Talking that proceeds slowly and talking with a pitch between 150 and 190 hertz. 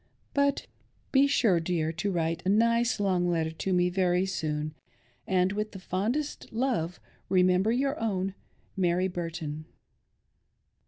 Yes: slow, 120 wpm; medium, 185 Hz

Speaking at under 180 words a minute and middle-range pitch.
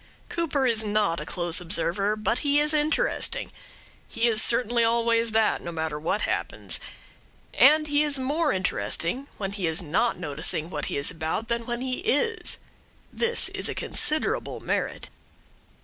No: average, 160 wpm; high, 230 Hz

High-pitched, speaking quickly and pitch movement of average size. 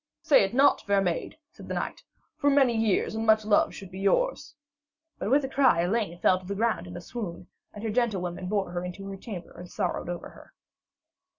Yes: high, 200 Hz; fast, 215 wpm; average, 4.5 semitones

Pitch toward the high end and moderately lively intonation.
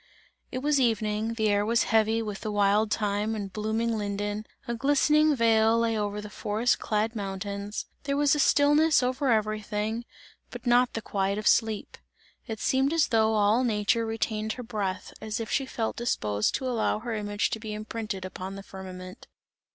No: high, 220 Hz; narrow, 2.3 semitones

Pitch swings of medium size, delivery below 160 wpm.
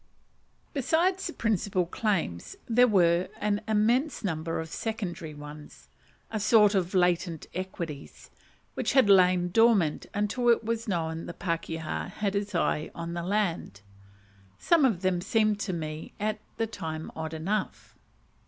Yes: average, 4.6 semitones; average, 145 wpm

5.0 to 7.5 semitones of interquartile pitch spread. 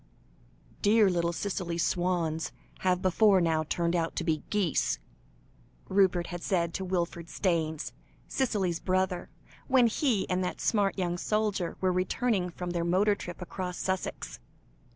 No: narrow, 2.4 semitones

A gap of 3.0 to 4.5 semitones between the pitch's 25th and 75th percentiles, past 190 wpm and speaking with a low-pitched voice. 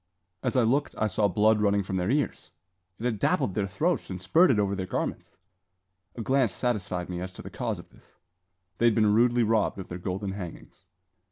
Yes: average, 3.9 semitones; fast, 205 wpm; low, 105 Hz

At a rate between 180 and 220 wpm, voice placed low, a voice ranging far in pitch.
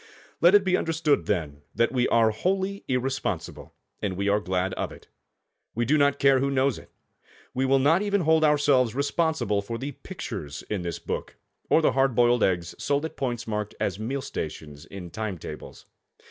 Yes: average, 190 wpm; low, 125 Hz; wide, 6.2 semitones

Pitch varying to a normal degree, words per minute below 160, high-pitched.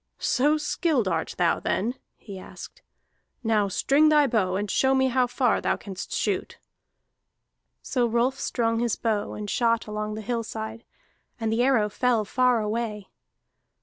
Yes: average, 3.0 semitones; average, 150 wpm; high, 230 Hz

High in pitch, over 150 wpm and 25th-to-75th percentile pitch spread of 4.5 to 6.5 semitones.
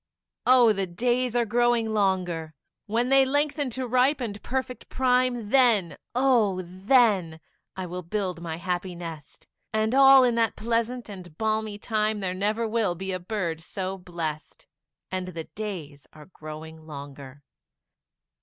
No: high, 205 Hz; average, 145 wpm; wide, 5.5 semitones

